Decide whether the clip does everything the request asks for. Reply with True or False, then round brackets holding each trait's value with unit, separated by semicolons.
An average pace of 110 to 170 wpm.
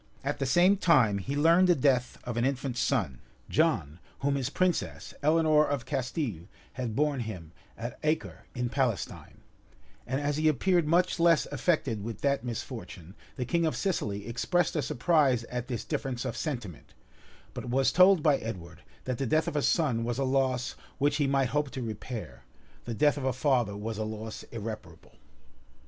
False (180 wpm)